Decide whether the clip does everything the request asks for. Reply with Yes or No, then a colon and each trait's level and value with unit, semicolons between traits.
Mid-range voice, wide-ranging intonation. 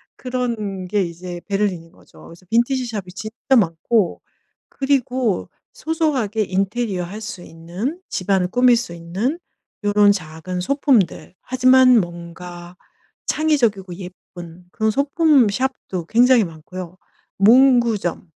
No: high, 205 Hz; wide, 5.8 semitones